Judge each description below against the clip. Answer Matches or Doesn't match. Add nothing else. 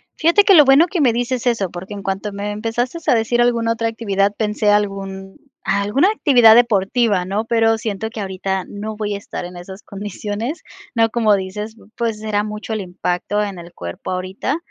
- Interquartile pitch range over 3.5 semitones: Doesn't match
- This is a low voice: Doesn't match